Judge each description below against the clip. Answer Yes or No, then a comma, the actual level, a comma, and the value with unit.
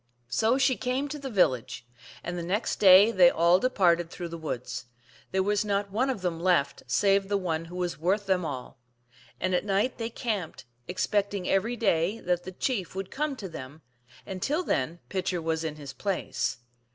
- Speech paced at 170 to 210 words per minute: Yes, average, 190 wpm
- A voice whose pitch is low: No, medium, 185 Hz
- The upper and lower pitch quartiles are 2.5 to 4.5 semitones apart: Yes, average, 3.7 semitones